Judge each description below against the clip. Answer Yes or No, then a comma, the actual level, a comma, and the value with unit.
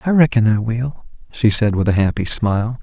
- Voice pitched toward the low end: Yes, low, 115 Hz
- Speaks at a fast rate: Yes, fast, 210 wpm